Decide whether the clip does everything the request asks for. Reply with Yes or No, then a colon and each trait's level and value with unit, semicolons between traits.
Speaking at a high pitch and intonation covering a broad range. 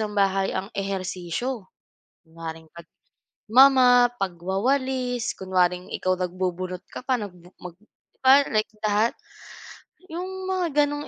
Yes: high, 205 Hz; wide, 5.8 semitones